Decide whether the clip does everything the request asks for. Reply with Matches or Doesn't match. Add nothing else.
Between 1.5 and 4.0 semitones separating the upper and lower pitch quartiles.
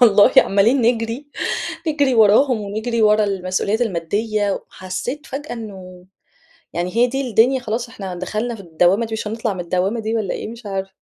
Matches